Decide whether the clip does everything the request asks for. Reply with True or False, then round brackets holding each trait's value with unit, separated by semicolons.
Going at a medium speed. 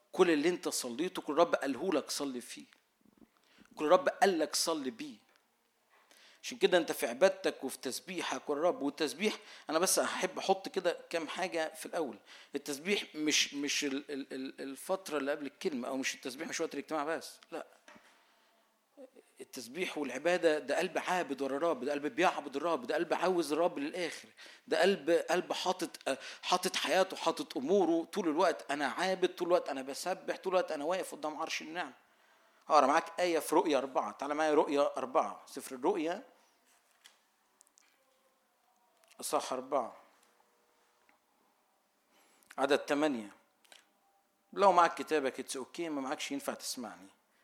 False (145 wpm)